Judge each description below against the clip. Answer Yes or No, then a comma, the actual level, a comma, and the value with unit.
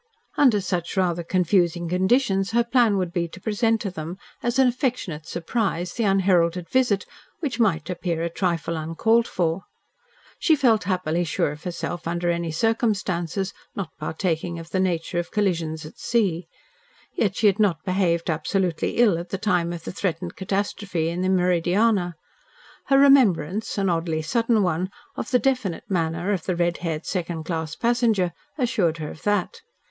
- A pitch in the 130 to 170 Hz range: No, medium, 180 Hz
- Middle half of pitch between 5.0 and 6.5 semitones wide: No, average, 3.9 semitones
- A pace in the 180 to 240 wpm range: No, average, 165 wpm